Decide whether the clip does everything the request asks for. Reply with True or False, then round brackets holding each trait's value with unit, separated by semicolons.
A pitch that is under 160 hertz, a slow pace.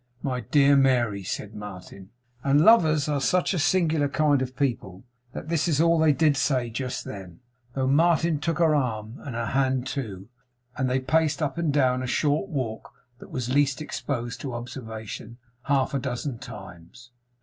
False (135 Hz; 175 wpm)